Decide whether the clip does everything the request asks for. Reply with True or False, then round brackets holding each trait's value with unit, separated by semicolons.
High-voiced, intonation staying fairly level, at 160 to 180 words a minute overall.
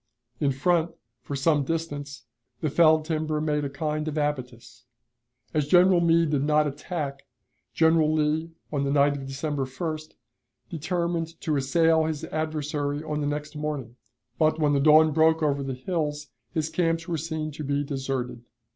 False (150 Hz; 2.1 semitones; 165 wpm)